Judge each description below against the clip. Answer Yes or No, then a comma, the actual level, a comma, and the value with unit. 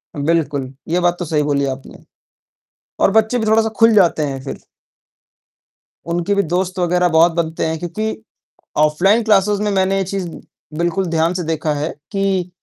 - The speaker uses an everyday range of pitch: Yes, average, 3.6 semitones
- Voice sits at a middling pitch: Yes, medium, 175 Hz